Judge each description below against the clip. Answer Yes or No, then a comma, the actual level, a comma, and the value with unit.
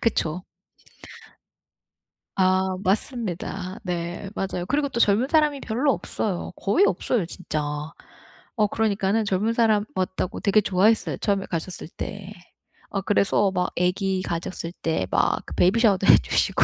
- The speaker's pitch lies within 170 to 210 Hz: Yes, high, 195 Hz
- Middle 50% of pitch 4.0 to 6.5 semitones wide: No, average, 3.2 semitones